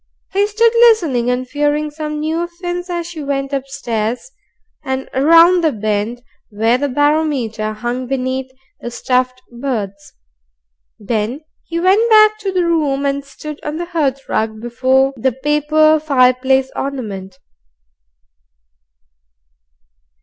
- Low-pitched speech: No, very high, 275 Hz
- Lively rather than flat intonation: No, average, 4.4 semitones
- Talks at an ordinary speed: No, slow, 120 wpm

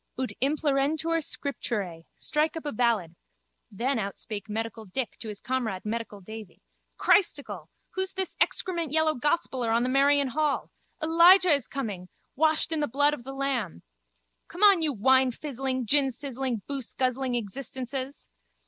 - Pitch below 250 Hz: No, very high, 265 Hz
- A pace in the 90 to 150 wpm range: Yes, average, 140 wpm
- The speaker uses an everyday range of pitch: Yes, average, 4.8 semitones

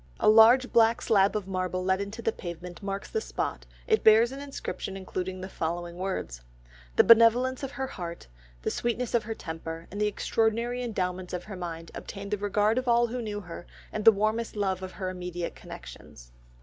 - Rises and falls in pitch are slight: No, average, 4.1 semitones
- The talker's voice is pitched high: Yes, high, 205 Hz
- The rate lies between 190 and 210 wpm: Yes, average, 195 wpm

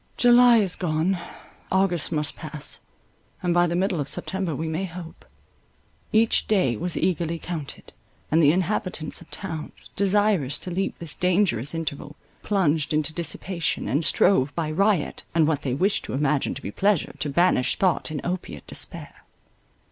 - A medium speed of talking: Yes, average, 160 wpm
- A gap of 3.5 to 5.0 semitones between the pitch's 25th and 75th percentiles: Yes, average, 3.8 semitones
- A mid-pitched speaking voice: Yes, medium, 170 Hz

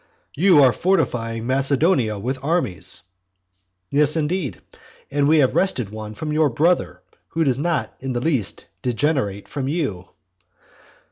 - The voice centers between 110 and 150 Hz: Yes, low, 135 Hz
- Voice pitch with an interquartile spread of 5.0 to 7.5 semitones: Yes, wide, 5.5 semitones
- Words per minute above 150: No, slow, 135 wpm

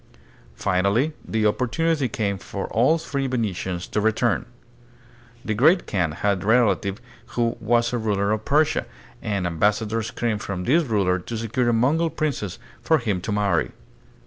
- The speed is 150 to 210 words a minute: Yes, average, 155 wpm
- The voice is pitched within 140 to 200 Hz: No, low, 110 Hz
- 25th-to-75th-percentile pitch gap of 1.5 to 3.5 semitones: No, average, 4.0 semitones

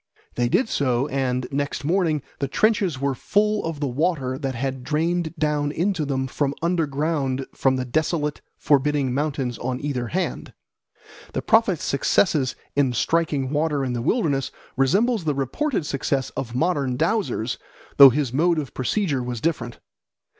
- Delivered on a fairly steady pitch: No, average, 4.0 semitones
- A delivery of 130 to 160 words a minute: Yes, average, 150 wpm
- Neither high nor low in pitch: Yes, medium, 145 Hz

